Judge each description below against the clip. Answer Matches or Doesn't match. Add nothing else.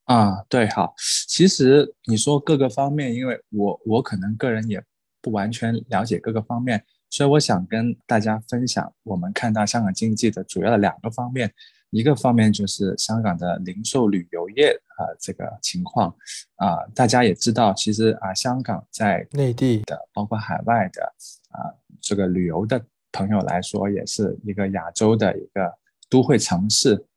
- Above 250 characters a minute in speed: Matches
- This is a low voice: Matches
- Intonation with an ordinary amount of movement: Matches